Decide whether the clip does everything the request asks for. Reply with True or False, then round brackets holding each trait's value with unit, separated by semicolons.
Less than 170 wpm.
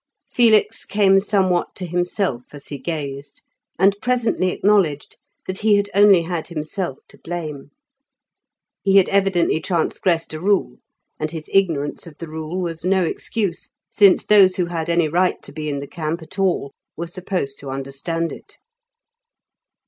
True (155 wpm)